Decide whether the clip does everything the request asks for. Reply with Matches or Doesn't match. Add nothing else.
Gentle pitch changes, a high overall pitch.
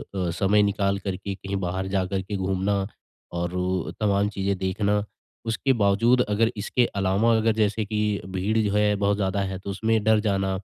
Doesn't match